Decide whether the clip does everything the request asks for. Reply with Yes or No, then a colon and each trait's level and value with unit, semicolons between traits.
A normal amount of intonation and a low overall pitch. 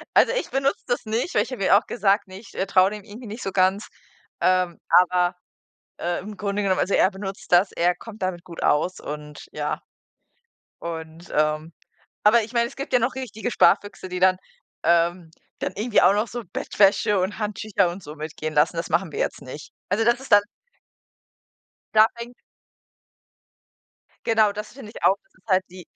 No: average, 3.6 semitones; high, 195 Hz